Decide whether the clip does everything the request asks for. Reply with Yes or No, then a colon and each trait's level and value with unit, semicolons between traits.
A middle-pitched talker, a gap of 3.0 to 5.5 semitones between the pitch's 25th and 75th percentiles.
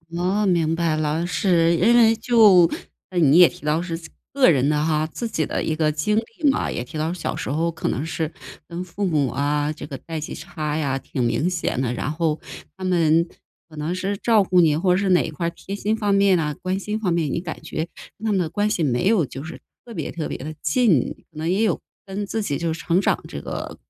Yes: medium, 170 Hz; average, 3.9 semitones